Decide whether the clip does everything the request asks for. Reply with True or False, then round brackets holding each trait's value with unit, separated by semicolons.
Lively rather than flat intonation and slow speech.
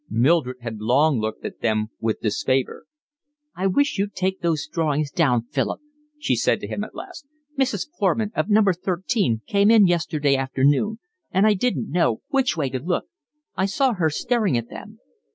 False (7.5 semitones; 175 wpm)